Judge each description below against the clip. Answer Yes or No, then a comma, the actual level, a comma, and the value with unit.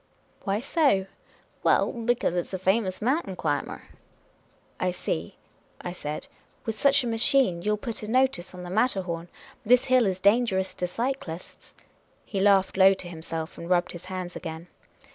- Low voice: No, high, 190 Hz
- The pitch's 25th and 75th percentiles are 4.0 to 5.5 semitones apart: Yes, average, 4.7 semitones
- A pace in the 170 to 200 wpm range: Yes, average, 185 wpm